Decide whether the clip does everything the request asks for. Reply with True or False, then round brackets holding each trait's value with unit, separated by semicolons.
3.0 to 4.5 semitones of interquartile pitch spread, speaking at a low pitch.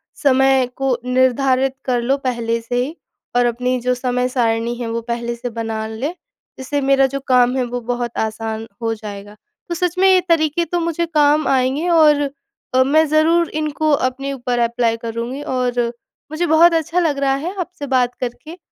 False (4.2 semitones; 260 Hz)